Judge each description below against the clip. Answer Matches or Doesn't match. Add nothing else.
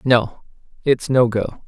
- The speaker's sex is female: Doesn't match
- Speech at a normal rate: Matches